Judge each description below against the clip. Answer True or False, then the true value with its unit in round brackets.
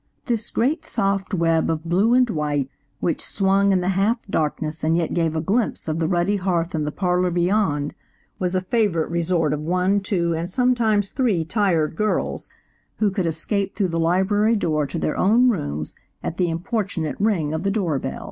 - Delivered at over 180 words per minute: True (190 wpm)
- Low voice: False (180 Hz)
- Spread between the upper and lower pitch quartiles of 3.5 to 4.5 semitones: True (3.9 semitones)